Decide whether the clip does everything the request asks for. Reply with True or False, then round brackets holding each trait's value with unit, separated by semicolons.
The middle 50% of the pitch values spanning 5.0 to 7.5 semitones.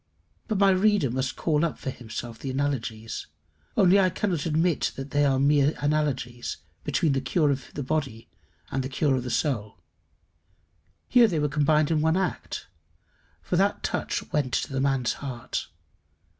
False (3.4 semitones)